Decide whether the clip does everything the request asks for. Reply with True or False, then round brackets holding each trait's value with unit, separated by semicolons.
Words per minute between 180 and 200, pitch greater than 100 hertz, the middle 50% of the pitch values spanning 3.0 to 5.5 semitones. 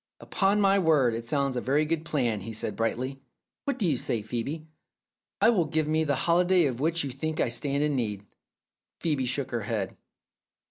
True (195 wpm; 140 Hz; 5.0 semitones)